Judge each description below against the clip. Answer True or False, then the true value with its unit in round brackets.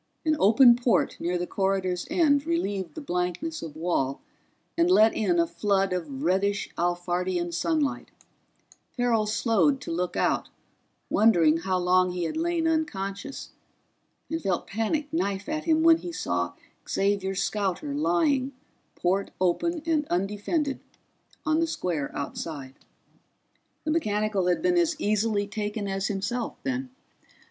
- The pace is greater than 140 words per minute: False (135 wpm)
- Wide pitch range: True (8.4 semitones)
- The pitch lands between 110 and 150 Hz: False (205 Hz)